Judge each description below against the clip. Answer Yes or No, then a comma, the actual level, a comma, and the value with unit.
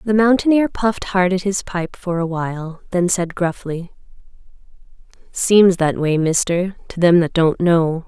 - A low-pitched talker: No, medium, 180 Hz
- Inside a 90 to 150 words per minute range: No, average, 165 wpm